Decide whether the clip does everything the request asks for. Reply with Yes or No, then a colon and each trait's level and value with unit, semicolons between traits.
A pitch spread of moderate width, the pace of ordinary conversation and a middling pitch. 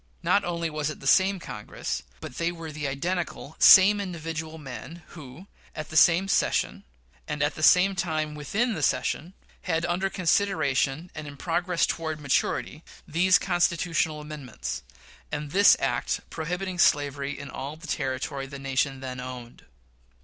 Yes: average, 3.7 semitones; average, 155 wpm; medium, 155 Hz